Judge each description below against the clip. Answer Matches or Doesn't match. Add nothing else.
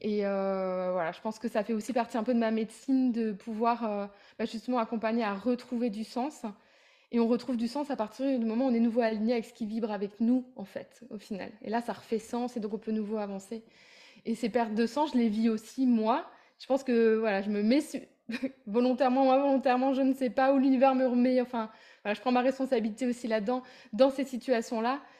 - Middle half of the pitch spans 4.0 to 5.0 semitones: Doesn't match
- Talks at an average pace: Doesn't match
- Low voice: Doesn't match